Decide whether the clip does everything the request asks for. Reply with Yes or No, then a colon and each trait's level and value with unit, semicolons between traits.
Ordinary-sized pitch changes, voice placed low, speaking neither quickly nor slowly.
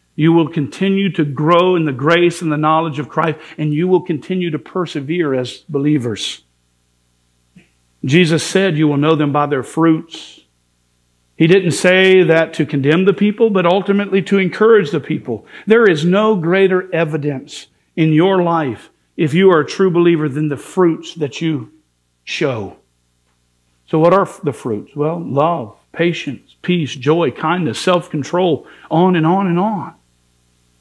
No: average, 4.3 semitones; medium, 160 Hz; average, 160 wpm